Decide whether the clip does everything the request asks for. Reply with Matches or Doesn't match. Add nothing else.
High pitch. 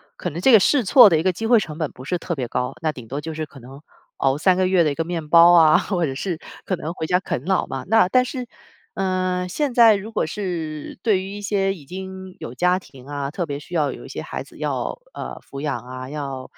Doesn't match